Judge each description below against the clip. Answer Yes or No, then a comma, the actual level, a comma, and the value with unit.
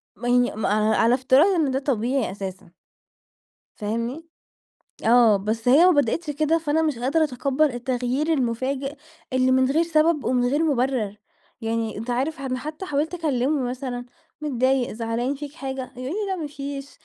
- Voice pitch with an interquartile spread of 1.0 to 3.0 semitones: No, average, 3.6 semitones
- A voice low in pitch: No, very high, 260 Hz